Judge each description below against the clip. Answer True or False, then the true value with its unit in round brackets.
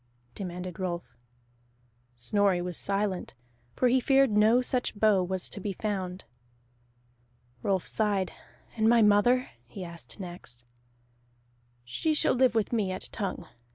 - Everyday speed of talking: False (130 wpm)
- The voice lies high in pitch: True (200 Hz)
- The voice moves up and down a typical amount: True (3.5 semitones)